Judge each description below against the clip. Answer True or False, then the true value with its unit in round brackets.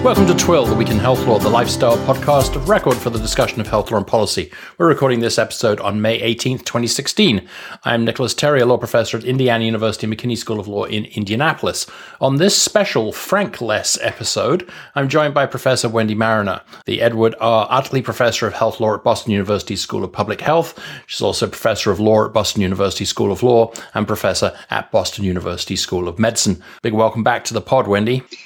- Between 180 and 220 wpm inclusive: True (200 wpm)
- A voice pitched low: True (115 Hz)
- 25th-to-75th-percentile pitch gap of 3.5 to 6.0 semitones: False (2.5 semitones)